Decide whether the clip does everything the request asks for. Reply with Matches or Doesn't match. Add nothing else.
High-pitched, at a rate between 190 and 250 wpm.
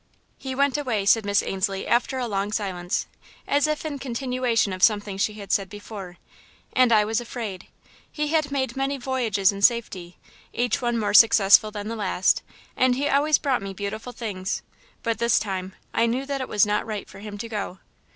Matches